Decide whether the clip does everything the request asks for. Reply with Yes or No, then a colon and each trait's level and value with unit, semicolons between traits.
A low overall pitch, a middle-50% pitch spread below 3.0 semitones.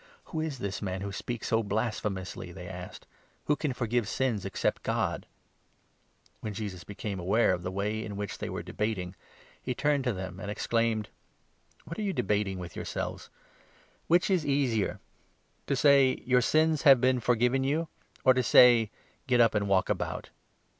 No: low, 115 Hz; average, 4.9 semitones